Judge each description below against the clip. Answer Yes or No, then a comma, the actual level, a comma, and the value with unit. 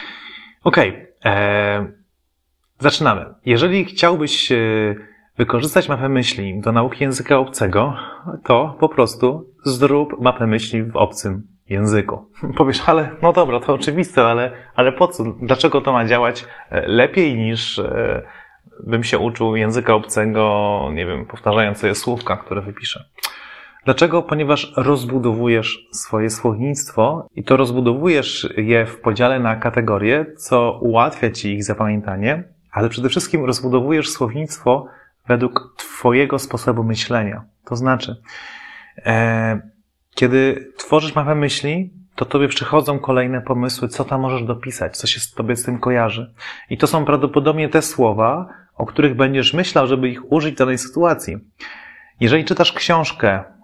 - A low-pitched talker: Yes, low, 125 Hz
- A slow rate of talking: No, average, 135 wpm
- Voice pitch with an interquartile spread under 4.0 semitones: No, average, 4.3 semitones